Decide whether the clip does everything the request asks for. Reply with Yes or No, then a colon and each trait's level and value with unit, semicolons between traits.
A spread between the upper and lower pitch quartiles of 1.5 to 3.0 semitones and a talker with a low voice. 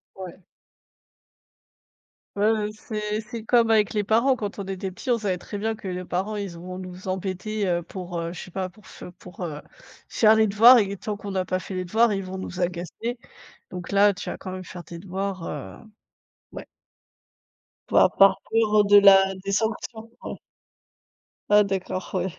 No: narrow, 2.6 semitones; high, 195 Hz